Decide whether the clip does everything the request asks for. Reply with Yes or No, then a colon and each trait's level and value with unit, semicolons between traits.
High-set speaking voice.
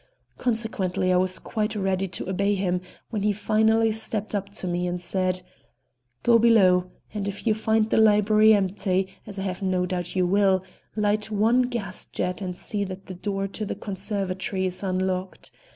Yes: high, 195 Hz